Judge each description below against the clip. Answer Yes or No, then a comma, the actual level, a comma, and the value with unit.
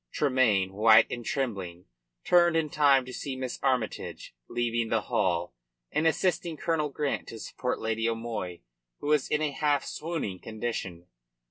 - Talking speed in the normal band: Yes, average, 150 wpm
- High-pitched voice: No, low, 125 Hz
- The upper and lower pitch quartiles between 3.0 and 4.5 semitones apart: No, average, 5.3 semitones